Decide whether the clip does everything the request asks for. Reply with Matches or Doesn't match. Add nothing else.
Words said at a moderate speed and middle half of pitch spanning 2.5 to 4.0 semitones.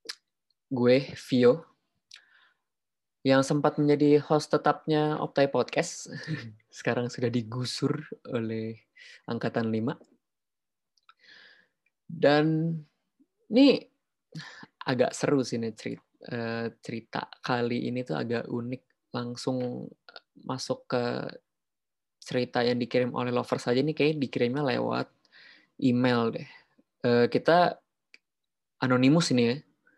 Matches